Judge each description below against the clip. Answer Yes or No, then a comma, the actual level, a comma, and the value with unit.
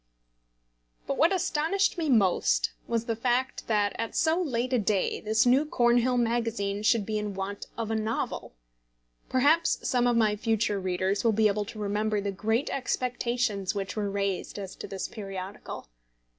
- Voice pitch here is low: No, high, 220 Hz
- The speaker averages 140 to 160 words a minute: No, average, 170 wpm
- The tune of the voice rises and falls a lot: No, average, 3.4 semitones